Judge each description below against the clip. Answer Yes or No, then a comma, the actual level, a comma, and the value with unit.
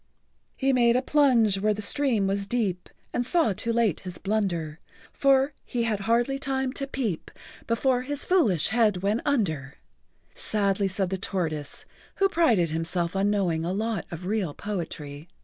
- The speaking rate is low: No, average, 165 wpm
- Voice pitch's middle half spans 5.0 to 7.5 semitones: Yes, wide, 5.5 semitones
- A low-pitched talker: No, high, 210 Hz